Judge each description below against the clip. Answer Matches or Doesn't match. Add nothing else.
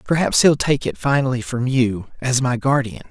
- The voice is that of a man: Matches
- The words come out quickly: Doesn't match